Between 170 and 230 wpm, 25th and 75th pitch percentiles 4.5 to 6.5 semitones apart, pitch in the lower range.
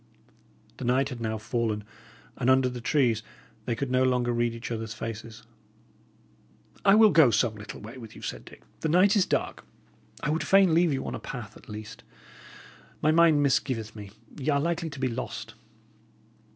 Yes: average, 185 wpm; average, 4.9 semitones; low, 125 Hz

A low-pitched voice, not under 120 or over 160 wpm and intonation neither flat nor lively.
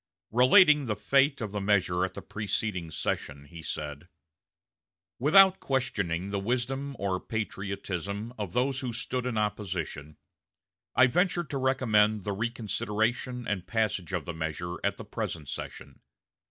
No: low, 105 Hz; average, 140 wpm; wide, 5.8 semitones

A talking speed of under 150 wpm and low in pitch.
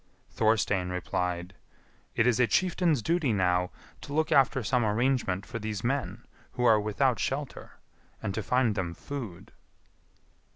Yes: average, 140 wpm; low, 115 Hz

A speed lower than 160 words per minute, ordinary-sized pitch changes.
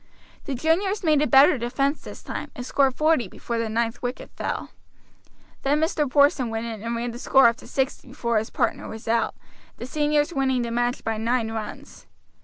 No: average, 200 wpm; average, 3.7 semitones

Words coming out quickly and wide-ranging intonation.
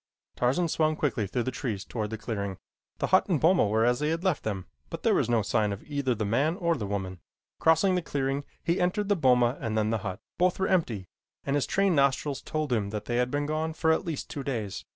Yes: fast, 245 wpm; wide, 6.6 semitones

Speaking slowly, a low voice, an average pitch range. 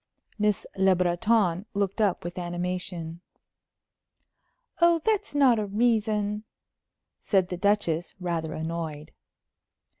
No: slow, 100 wpm; high, 190 Hz; average, 3.5 semitones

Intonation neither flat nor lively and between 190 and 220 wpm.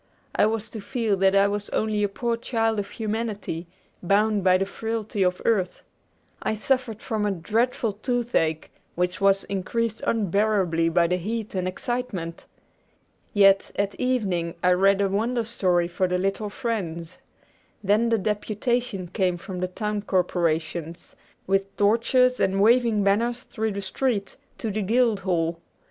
No: average, 3.5 semitones; average, 155 wpm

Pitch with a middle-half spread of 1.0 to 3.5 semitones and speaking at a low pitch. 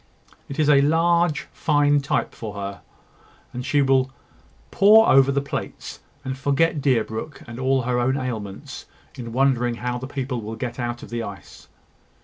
Yes: average, 2.8 semitones; low, 130 Hz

